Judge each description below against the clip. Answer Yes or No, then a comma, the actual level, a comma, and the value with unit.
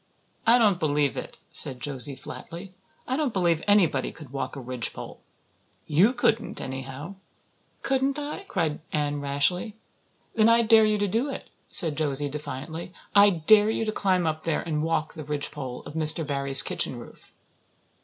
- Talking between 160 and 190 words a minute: Yes, average, 165 wpm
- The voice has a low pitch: No, medium, 160 Hz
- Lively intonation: Yes, wide, 6.5 semitones